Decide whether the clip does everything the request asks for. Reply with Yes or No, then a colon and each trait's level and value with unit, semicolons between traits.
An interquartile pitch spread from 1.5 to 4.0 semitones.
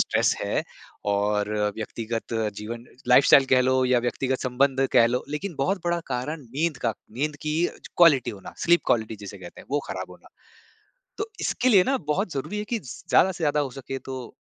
No: average, 4.8 semitones